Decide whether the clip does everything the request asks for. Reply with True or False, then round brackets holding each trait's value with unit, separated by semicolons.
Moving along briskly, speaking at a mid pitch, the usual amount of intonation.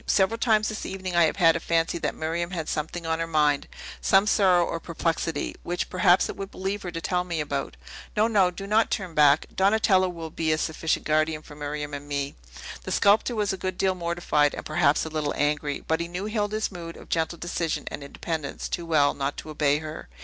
True (220 wpm; 165 Hz; 3.5 semitones)